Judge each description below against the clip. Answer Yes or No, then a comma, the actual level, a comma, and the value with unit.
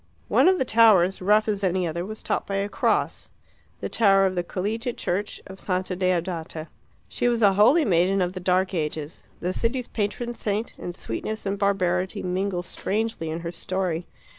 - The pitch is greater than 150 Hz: Yes, high, 190 Hz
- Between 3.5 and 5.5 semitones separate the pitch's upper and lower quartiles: No, average, 3.0 semitones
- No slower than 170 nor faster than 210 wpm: Yes, average, 185 wpm